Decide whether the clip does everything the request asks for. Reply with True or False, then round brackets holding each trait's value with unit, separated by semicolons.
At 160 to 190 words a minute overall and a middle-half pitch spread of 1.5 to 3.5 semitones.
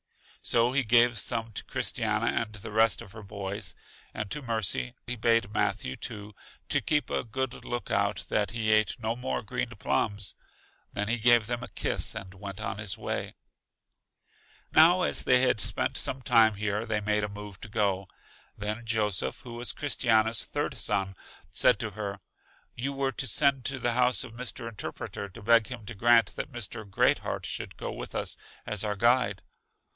True (180 wpm; 2.7 semitones)